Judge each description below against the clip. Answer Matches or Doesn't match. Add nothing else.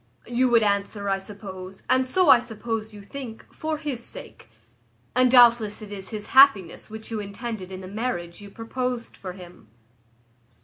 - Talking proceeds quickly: Doesn't match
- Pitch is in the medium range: Doesn't match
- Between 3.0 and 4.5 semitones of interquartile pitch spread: Matches